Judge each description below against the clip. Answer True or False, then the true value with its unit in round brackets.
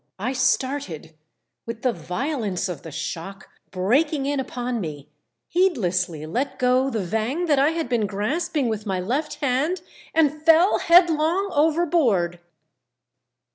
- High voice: True (255 Hz)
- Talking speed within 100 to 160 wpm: True (135 wpm)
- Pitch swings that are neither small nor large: False (7.9 semitones)